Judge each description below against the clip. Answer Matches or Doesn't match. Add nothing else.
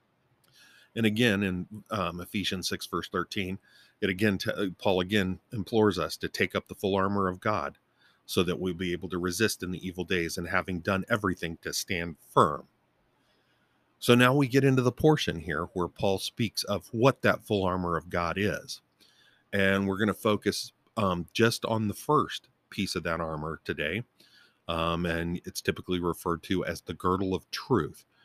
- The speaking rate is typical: Matches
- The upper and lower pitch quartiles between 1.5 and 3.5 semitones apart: Matches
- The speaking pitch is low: Matches